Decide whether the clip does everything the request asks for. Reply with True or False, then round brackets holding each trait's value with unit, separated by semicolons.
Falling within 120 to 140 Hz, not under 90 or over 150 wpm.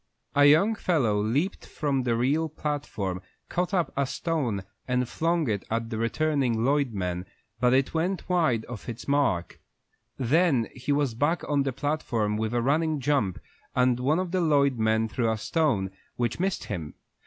False (135 Hz; 175 wpm)